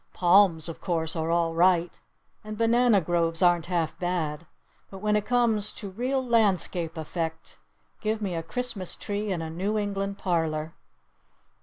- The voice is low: No, medium, 185 Hz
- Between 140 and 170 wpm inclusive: Yes, average, 155 wpm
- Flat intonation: No, average, 4.2 semitones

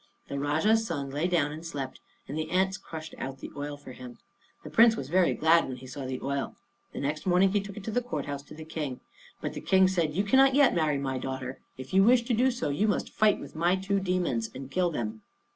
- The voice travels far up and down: Yes, wide, 5.7 semitones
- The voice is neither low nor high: Yes, medium, 160 Hz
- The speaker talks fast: Yes, fast, 250 wpm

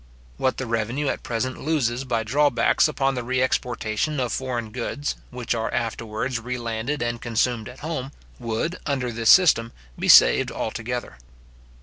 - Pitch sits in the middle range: No, low, 125 Hz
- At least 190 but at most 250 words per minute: No, average, 155 wpm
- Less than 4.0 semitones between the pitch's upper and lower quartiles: Yes, narrow, 2.5 semitones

